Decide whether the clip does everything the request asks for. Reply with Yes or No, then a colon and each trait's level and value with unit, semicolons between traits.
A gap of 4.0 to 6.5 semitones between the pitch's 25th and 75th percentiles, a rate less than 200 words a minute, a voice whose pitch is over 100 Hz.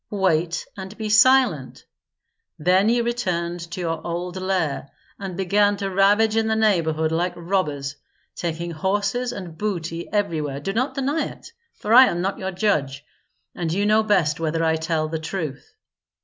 Yes: average, 4.3 semitones; average, 165 wpm; medium, 185 Hz